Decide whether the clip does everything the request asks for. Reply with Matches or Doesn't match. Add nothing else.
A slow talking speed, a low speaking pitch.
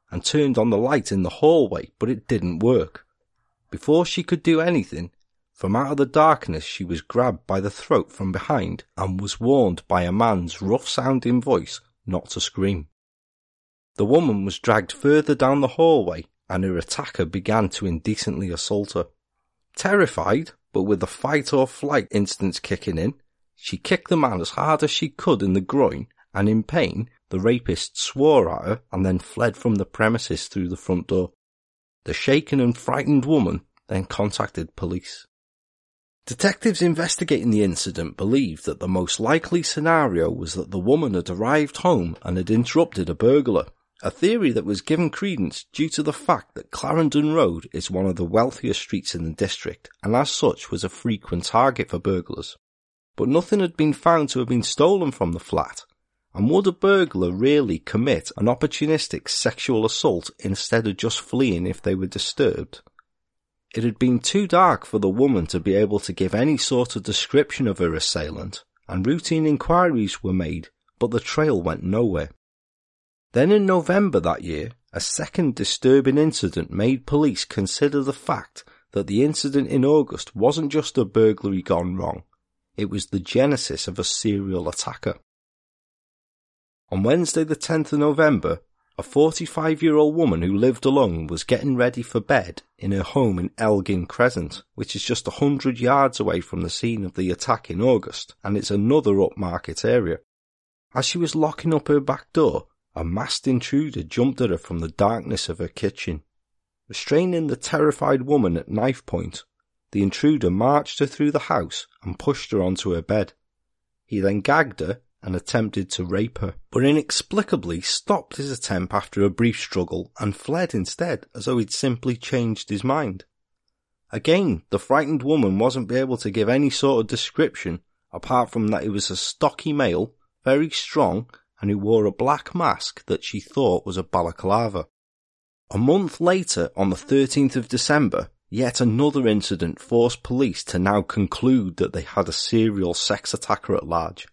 Doesn't match